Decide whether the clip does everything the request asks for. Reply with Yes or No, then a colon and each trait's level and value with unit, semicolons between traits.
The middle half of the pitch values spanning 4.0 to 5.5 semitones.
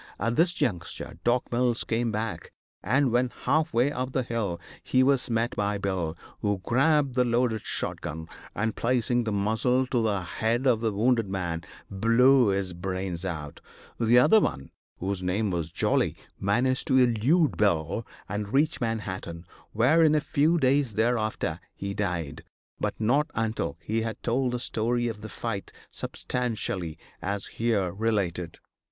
Yes: average, 4.4 semitones